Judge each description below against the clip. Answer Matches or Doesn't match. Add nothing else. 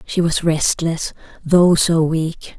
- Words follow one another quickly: Doesn't match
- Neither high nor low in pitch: Matches